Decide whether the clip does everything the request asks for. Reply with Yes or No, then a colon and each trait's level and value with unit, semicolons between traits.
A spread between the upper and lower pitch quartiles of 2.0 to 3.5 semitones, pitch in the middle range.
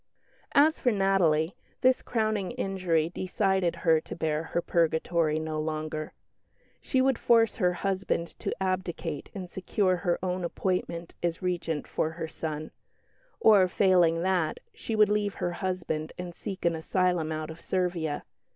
Yes: average, 3.1 semitones; medium, 180 Hz